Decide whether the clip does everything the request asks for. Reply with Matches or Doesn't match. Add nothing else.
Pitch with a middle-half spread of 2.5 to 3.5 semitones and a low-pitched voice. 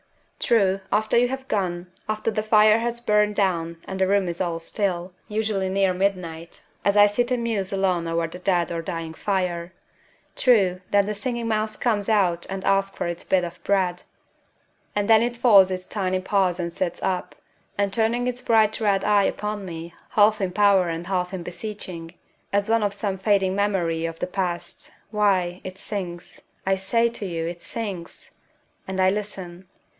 Doesn't match